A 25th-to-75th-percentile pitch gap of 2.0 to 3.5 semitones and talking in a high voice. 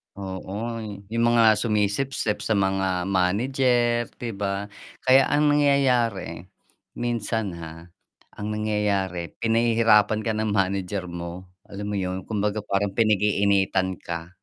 No: average, 3.2 semitones; low, 105 Hz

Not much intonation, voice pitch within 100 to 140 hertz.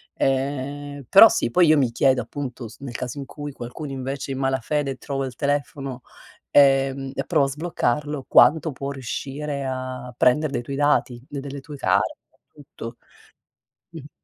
Yes: narrow, 1.8 semitones; low, 135 Hz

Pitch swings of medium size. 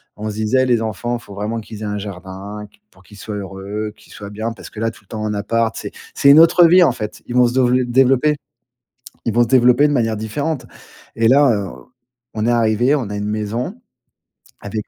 Yes: average, 3.2 semitones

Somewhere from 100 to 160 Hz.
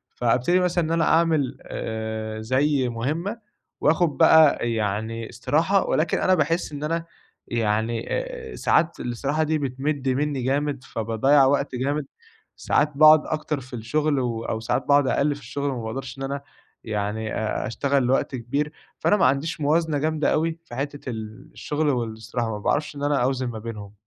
Yes: medium, 140 Hz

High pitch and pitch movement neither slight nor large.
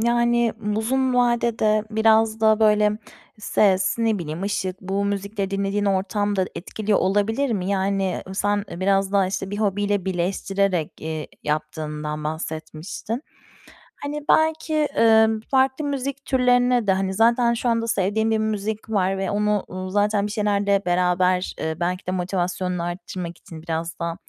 Yes: high, 200 Hz; average, 3.2 semitones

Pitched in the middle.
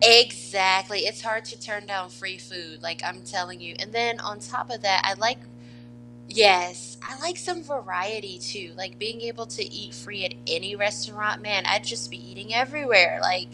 No: high, 195 Hz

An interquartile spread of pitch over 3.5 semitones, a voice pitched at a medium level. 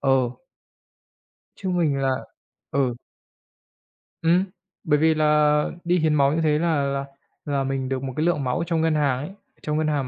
No: narrow, 2.6 semitones; medium, 150 Hz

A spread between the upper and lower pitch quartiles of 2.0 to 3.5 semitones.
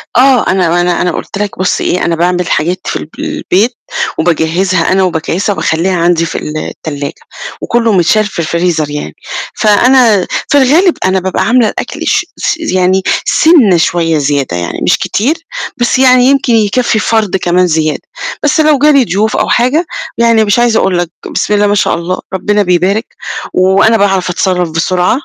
No: average, 5.0 semitones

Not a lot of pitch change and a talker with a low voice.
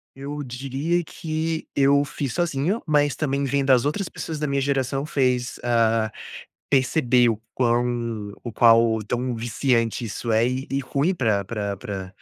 No: average, 3.4 semitones; low, 130 Hz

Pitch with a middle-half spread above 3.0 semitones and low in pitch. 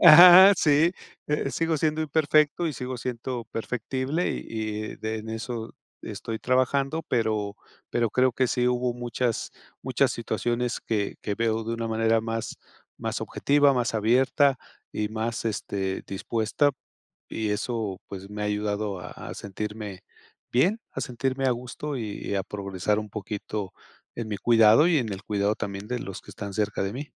Yes: average, 3.7 semitones; low, 115 Hz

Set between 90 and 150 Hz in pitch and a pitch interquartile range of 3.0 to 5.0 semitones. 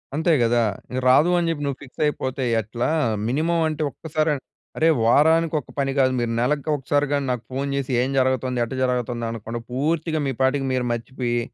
Yes: low, 135 Hz; average, 3.3 semitones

